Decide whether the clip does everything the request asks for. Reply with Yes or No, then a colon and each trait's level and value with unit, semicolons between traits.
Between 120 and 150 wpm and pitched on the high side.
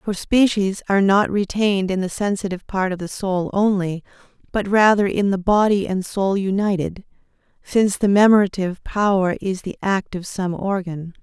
No: average, 165 wpm; high, 195 Hz